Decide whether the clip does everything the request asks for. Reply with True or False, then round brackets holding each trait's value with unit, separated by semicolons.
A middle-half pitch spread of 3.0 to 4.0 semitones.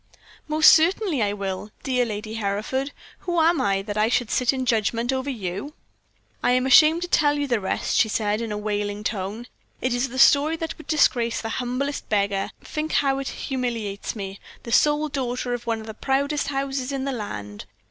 False (5.0 semitones)